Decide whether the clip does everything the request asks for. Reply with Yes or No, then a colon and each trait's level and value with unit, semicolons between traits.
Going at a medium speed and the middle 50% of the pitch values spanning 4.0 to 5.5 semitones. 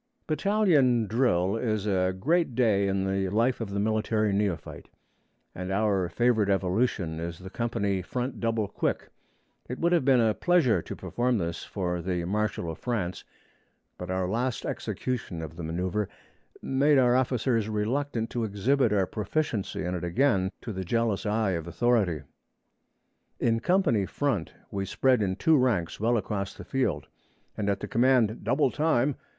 Yes: average, 160 wpm; average, 5.0 semitones